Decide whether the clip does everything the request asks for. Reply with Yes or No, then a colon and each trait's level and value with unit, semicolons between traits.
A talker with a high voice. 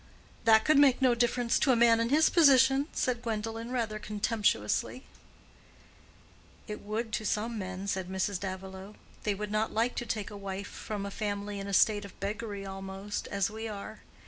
Yes: high, 215 Hz